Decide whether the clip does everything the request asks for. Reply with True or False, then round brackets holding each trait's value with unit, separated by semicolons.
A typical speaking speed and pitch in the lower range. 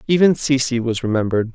True (155 wpm; 125 Hz)